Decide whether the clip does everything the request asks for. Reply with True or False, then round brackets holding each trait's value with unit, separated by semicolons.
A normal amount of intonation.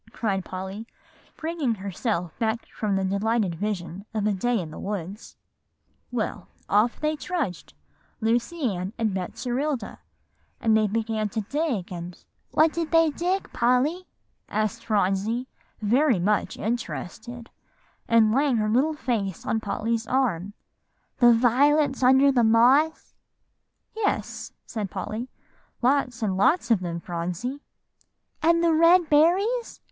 False (5.7 semitones)